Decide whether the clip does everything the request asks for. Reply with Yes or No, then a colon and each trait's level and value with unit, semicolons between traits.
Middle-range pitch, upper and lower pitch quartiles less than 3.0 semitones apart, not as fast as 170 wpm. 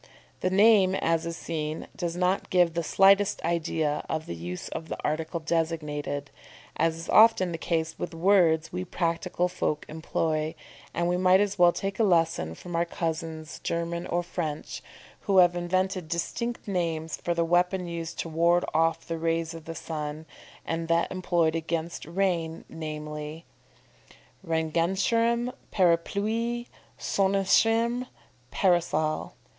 Yes: medium, 170 Hz; narrow, 2.4 semitones; average, 140 wpm